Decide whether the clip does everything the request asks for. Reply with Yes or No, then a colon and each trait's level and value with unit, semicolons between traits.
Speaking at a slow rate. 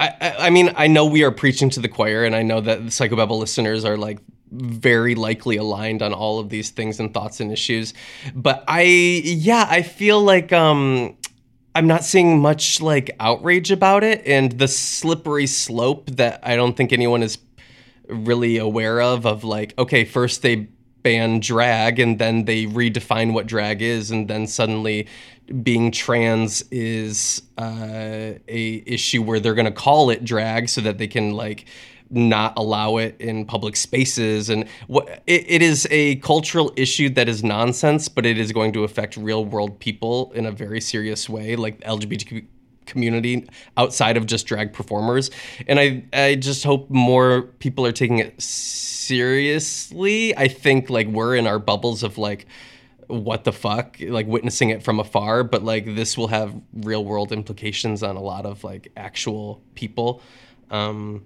No: average, 175 wpm